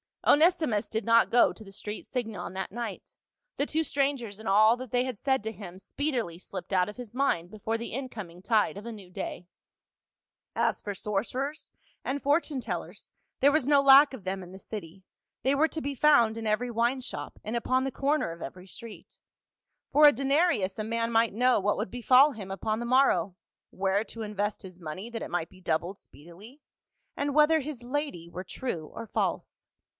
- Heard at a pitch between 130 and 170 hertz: No, high, 225 Hz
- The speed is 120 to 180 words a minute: No, average, 200 wpm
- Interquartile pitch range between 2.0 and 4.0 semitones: No, wide, 5.6 semitones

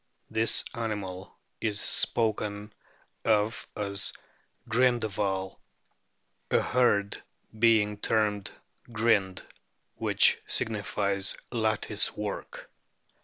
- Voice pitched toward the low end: Yes, low, 105 Hz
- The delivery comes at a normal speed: No, slow, 75 wpm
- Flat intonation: Yes, narrow, 1.9 semitones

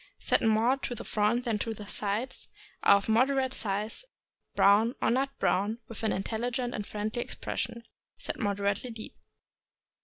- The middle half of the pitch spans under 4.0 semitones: Yes, average, 2.8 semitones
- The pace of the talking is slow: No, average, 160 wpm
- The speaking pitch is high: Yes, high, 220 Hz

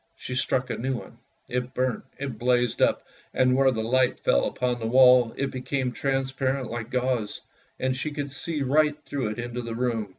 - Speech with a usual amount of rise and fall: No, narrow, 1.7 semitones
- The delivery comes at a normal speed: Yes, average, 195 wpm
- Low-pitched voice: Yes, low, 125 Hz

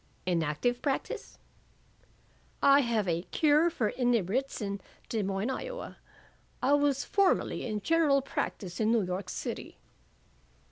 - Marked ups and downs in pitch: Yes, wide, 6.2 semitones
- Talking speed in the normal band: No, slow, 130 wpm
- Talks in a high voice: Yes, high, 240 Hz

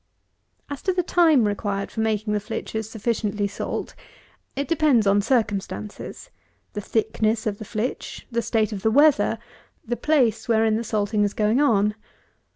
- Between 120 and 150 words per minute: No, average, 160 wpm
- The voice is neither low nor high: No, high, 220 Hz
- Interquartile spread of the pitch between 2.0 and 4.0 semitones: Yes, narrow, 2.5 semitones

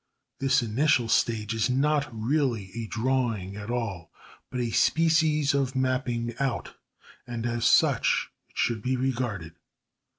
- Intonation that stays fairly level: No, average, 3.0 semitones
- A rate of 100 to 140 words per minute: Yes, slow, 135 wpm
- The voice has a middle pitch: No, low, 120 Hz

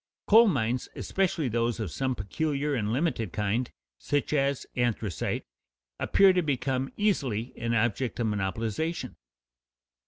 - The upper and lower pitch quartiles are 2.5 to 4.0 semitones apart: No, average, 4.8 semitones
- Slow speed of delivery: Yes, slow, 125 wpm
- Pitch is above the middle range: No, low, 125 Hz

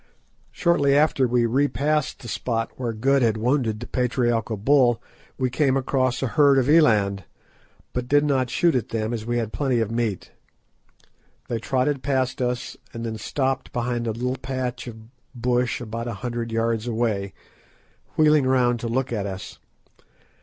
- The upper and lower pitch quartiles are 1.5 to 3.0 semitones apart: Yes, narrow, 2.6 semitones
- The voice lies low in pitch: Yes, low, 125 Hz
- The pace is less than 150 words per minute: No, average, 165 wpm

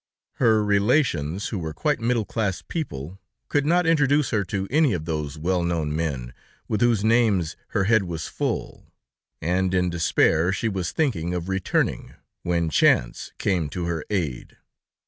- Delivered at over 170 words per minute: No, average, 160 wpm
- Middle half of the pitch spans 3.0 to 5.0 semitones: No, wide, 5.5 semitones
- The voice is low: Yes, very low, 95 Hz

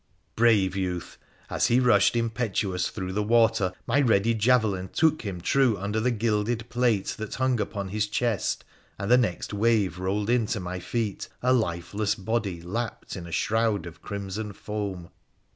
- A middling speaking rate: Yes, average, 165 wpm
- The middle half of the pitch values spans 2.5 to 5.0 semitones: Yes, average, 3.4 semitones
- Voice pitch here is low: Yes, low, 105 Hz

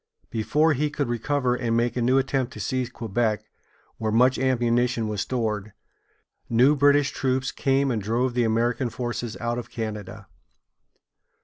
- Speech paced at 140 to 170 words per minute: Yes, average, 150 wpm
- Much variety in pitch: No, narrow, 2.5 semitones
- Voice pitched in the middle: No, low, 120 Hz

